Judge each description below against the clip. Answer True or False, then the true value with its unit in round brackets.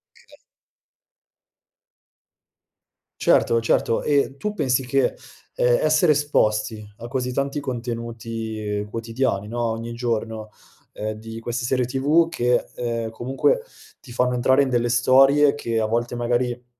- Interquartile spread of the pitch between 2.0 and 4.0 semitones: True (2.7 semitones)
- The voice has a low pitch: True (120 Hz)